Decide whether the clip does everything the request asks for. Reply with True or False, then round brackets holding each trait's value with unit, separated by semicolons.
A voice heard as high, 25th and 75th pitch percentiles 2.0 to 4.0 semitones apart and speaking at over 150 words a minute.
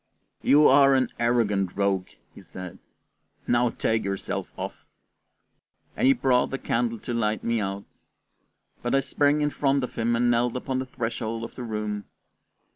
False (120 Hz; 3.5 semitones; 165 wpm)